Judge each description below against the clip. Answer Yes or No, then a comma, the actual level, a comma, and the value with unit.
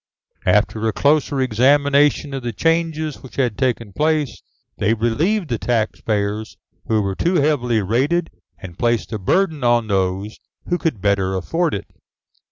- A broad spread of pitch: Yes, wide, 5.9 semitones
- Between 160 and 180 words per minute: No, average, 150 wpm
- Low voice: Yes, low, 120 Hz